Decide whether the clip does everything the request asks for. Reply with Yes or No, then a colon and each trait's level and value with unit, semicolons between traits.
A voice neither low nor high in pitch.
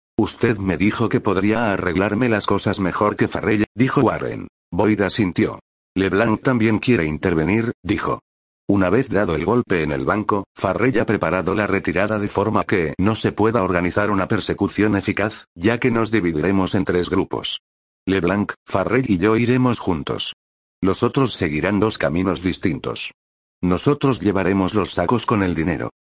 No: low, 100 Hz